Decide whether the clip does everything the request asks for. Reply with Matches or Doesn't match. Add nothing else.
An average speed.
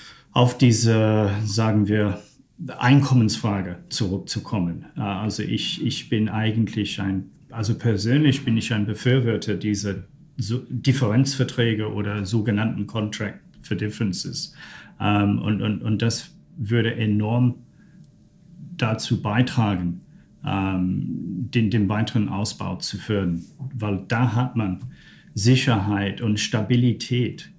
Doesn't match